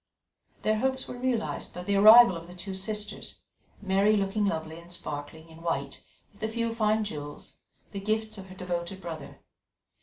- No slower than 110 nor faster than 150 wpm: No, average, 175 wpm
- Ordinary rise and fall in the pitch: Yes, average, 4.2 semitones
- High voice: Yes, high, 195 Hz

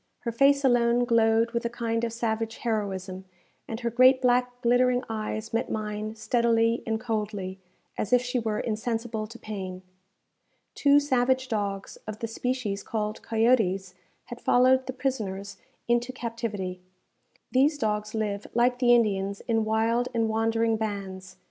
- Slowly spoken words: No, average, 150 wpm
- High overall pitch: Yes, high, 225 Hz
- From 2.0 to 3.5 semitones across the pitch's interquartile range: Yes, narrow, 2.5 semitones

